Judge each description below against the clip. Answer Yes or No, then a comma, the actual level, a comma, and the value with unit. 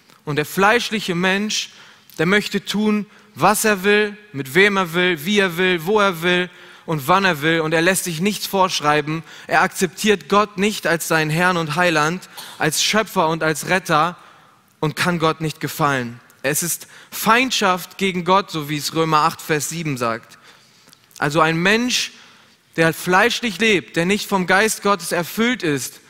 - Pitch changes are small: No, average, 4.1 semitones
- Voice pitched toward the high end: No, medium, 180 Hz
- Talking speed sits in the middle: Yes, average, 170 wpm